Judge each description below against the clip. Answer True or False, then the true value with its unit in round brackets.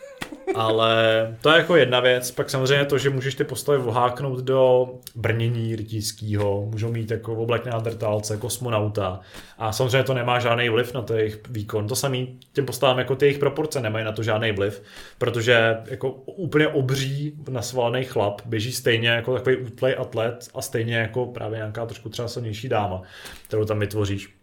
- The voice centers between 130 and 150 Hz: False (120 Hz)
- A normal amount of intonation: True (3.0 semitones)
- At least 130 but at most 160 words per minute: False (170 wpm)